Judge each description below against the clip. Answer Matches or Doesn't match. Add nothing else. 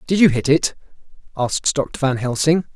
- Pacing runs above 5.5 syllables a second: Doesn't match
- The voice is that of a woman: Doesn't match